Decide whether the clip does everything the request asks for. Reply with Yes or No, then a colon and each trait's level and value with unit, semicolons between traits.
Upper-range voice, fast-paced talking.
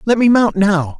Yes: high, 205 Hz; fast, 240 wpm